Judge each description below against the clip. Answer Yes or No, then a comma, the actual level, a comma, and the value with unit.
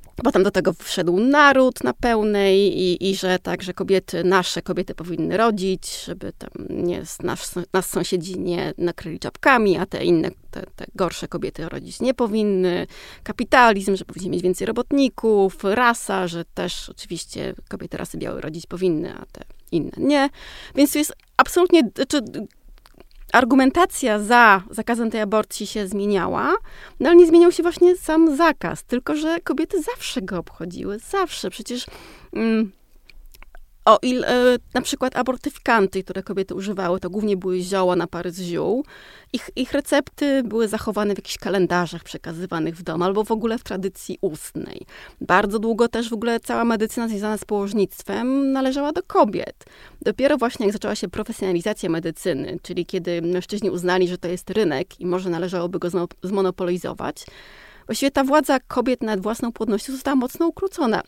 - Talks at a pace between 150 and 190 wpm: Yes, fast, 160 wpm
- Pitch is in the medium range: No, high, 210 Hz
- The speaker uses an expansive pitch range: Yes, wide, 5.8 semitones